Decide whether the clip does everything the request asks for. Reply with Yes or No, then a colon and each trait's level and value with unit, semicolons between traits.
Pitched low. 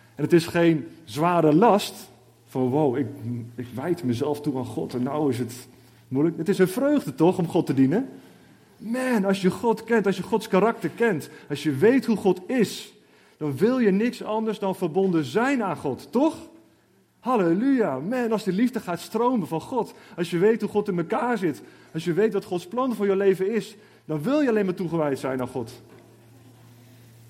No: medium, 180 Hz